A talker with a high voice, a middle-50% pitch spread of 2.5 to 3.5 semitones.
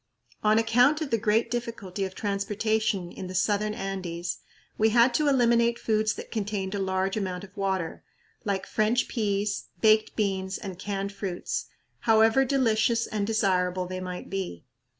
Yes: high, 205 Hz; average, 2.8 semitones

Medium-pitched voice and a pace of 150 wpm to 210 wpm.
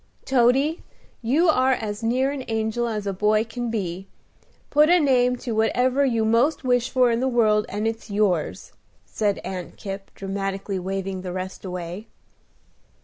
No: high, 225 Hz; average, 160 wpm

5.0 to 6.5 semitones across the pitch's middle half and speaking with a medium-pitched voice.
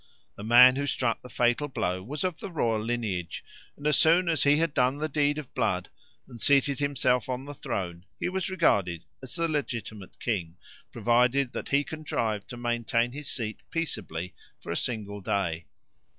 No: average, 5.3 semitones; low, 125 Hz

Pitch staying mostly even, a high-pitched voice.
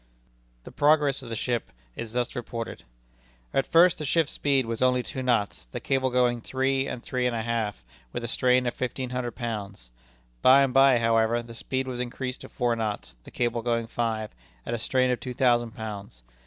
No: narrow, 2.2 semitones; low, 120 Hz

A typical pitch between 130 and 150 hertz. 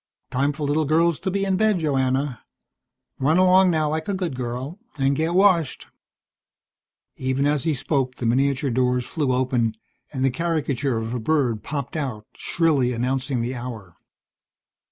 Yes: medium, 140 Hz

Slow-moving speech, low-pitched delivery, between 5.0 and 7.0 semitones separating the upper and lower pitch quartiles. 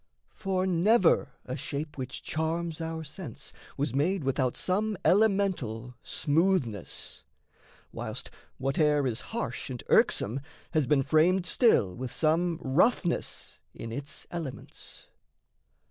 No: slow, 115 wpm; medium, 155 Hz; wide, 5.5 semitones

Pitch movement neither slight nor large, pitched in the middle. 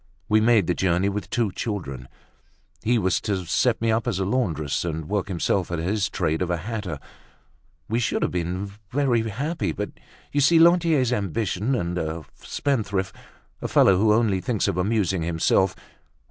No: average, 4.7 semitones; low, 100 Hz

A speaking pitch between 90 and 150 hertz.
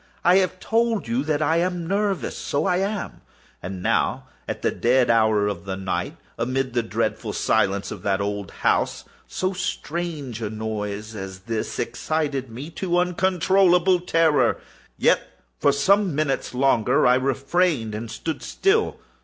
Yes: medium, 140 Hz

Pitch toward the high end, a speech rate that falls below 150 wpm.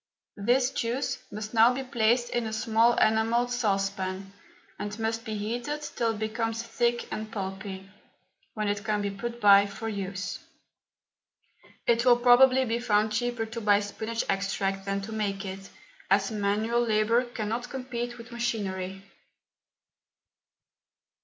Yes: high, 220 Hz; average, 140 wpm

